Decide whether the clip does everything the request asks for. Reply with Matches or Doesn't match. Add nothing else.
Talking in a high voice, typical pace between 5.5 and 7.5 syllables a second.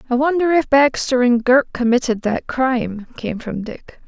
Doesn't match